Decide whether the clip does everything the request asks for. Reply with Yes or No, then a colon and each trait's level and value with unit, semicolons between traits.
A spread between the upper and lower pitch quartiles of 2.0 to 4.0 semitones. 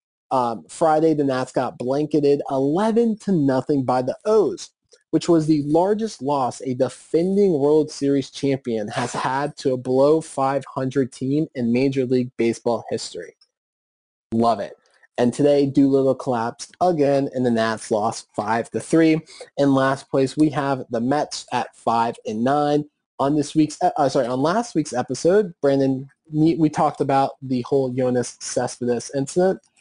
Yes: average, 3.2 semitones